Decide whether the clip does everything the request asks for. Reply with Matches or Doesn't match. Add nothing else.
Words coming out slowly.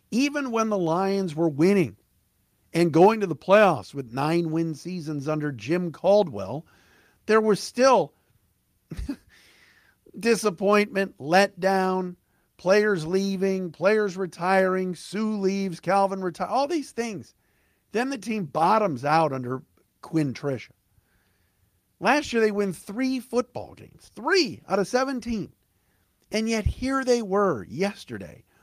Matches